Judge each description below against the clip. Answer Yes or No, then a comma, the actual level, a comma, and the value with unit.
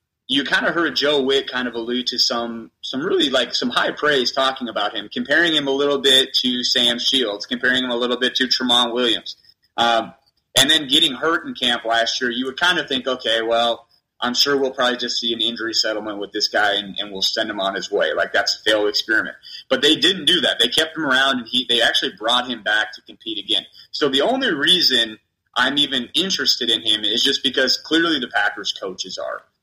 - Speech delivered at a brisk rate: Yes, fast, 230 wpm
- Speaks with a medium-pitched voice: No, low, 125 Hz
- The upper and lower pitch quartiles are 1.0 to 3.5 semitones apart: Yes, average, 2.8 semitones